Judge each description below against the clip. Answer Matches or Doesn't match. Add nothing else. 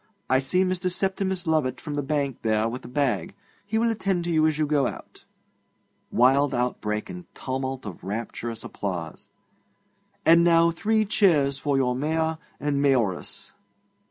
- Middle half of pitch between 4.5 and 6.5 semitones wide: Matches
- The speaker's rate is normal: Matches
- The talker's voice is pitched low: Doesn't match